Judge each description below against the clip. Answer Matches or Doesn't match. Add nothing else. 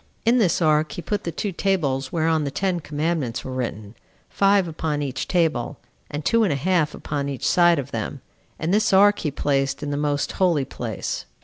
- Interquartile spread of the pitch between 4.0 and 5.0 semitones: Matches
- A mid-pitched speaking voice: Matches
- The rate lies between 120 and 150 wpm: Doesn't match